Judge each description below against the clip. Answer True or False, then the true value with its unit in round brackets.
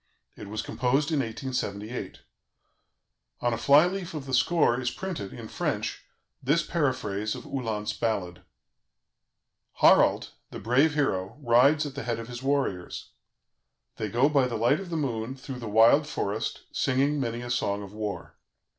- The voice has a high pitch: False (125 Hz)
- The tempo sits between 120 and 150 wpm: False (160 wpm)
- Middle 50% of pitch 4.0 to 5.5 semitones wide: True (4.5 semitones)